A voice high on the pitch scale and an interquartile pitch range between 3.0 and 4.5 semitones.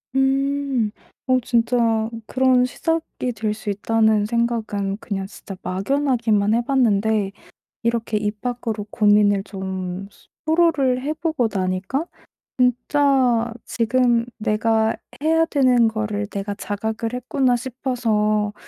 Yes: high, 230 Hz; average, 3.5 semitones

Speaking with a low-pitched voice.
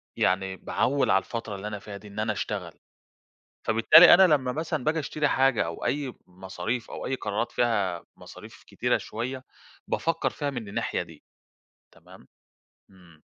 Yes: low, 115 Hz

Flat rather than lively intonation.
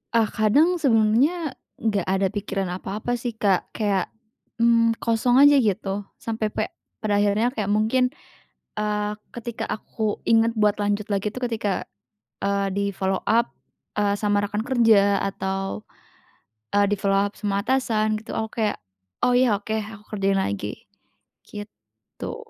Yes: narrow, 2.3 semitones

